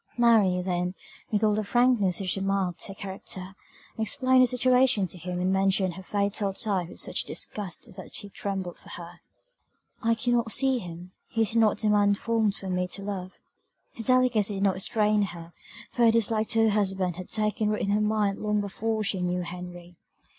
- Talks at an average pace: Yes, average, 190 wpm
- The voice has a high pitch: Yes, high, 200 Hz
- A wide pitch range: No, average, 3.2 semitones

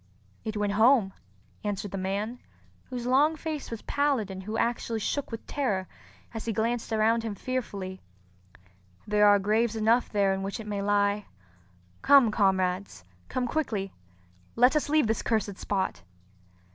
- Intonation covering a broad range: No, average, 3.3 semitones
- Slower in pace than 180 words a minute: Yes, average, 150 wpm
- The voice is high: Yes, high, 215 Hz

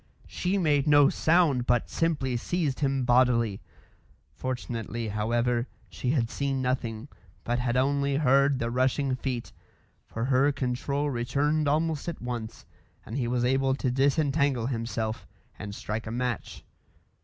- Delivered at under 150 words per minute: Yes, average, 140 wpm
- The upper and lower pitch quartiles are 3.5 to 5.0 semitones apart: No, average, 2.9 semitones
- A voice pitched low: Yes, low, 130 Hz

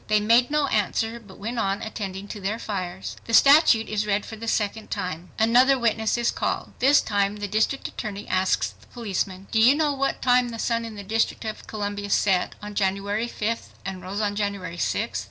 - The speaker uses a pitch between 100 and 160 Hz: No, high, 215 Hz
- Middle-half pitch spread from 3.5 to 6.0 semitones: No, narrow, 2.5 semitones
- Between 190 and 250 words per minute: Yes, average, 200 wpm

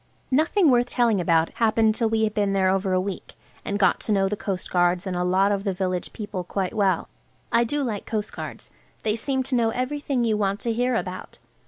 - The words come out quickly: Yes, fast, 220 wpm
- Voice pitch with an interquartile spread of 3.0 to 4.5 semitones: Yes, average, 3.7 semitones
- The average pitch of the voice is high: Yes, high, 210 Hz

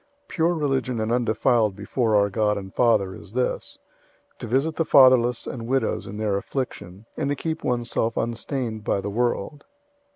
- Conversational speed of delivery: Yes, average, 170 wpm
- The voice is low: Yes, low, 120 Hz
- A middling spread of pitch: Yes, average, 4.0 semitones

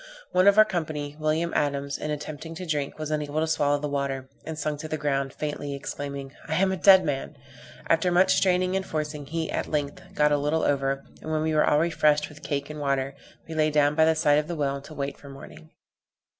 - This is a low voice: No, medium, 150 Hz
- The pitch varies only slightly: Yes, narrow, 2.1 semitones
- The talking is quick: Yes, fast, 235 wpm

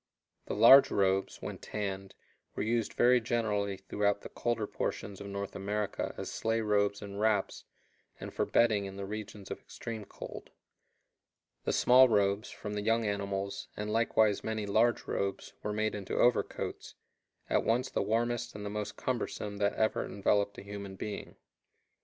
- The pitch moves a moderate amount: No, narrow, 1.9 semitones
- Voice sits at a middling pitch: No, low, 105 Hz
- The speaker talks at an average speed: Yes, average, 165 wpm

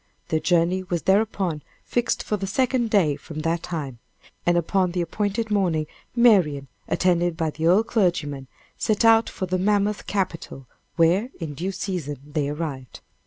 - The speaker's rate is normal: Yes, average, 160 wpm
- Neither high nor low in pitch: Yes, medium, 180 Hz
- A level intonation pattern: No, average, 4.3 semitones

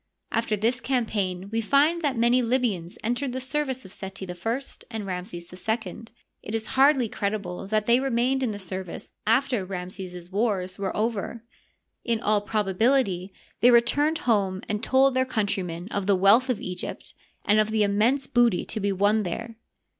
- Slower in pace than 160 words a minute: No, average, 170 wpm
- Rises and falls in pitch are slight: No, average, 4.3 semitones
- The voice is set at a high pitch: Yes, high, 220 Hz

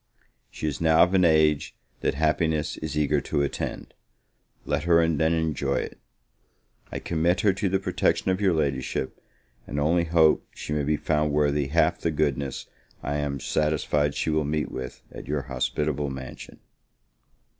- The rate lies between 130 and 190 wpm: Yes, average, 165 wpm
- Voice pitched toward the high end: No, very low, 75 Hz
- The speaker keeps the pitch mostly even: Yes, narrow, 2.2 semitones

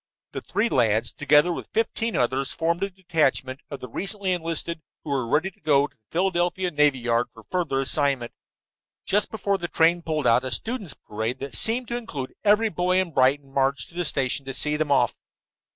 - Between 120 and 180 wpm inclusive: No, average, 195 wpm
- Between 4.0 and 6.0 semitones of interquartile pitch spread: Yes, wide, 5.5 semitones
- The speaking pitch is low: No, medium, 150 Hz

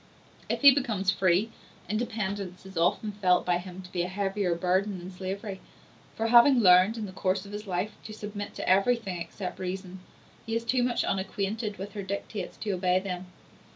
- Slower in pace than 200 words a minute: Yes, average, 190 wpm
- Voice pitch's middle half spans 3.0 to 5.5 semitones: No, narrow, 2.5 semitones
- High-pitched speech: Yes, high, 195 Hz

